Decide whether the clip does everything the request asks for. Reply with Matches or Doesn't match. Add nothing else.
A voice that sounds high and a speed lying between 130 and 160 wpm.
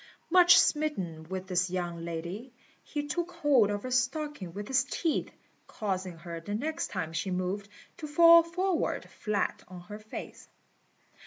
Matches